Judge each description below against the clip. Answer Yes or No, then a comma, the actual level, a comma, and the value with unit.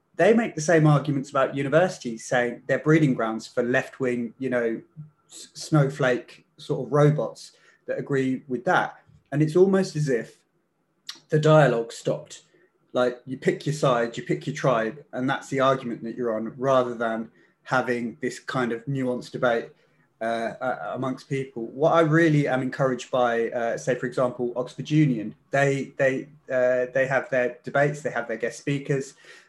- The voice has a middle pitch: No, low, 130 Hz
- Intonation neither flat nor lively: Yes, average, 3.0 semitones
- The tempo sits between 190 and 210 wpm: No, average, 170 wpm